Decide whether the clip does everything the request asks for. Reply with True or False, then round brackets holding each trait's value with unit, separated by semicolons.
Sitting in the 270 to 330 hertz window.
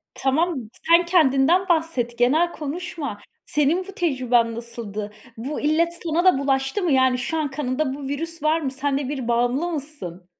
True (280 Hz)